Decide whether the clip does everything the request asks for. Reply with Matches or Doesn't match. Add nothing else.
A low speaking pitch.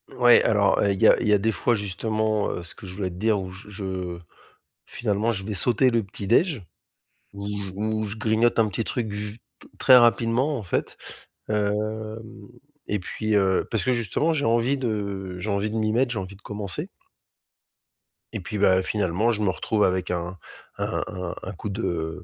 Matches